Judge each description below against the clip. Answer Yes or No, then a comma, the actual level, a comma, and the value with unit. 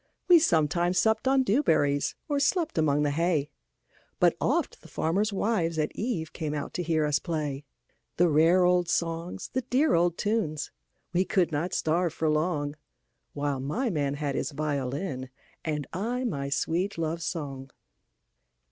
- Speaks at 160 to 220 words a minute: No, average, 140 wpm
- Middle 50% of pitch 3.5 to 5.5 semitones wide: Yes, average, 4.1 semitones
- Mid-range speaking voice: Yes, medium, 165 Hz